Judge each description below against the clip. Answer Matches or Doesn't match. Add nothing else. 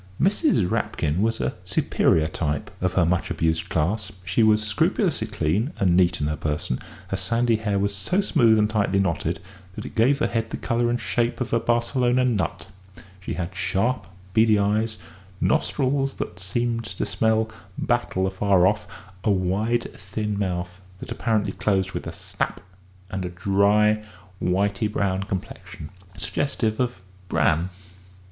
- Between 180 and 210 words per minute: Doesn't match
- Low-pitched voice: Matches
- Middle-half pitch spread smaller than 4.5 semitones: Matches